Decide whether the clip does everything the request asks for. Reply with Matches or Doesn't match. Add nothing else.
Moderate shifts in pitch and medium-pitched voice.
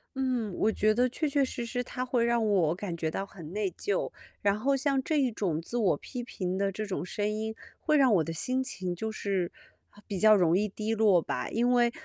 Doesn't match